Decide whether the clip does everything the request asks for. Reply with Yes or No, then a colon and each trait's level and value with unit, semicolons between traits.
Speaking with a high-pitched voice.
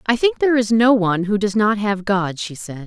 Yes: high, 210 Hz